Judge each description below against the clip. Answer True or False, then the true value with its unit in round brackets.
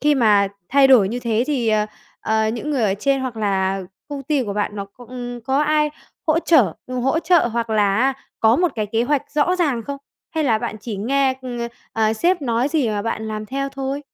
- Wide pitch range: False (4.3 semitones)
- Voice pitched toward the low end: False (245 Hz)